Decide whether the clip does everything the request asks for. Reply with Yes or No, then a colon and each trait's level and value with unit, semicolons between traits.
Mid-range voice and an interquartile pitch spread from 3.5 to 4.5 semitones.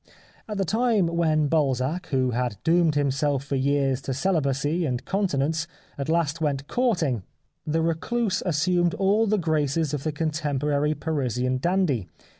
Yes: medium, 155 Hz; average, 4.0 semitones